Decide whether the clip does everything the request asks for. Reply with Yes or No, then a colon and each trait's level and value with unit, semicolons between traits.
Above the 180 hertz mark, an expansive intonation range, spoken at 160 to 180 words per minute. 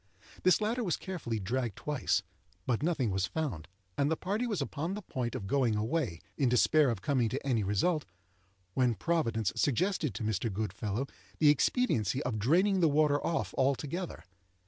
No: low, 135 Hz; wide, 6.7 semitones; average, 170 wpm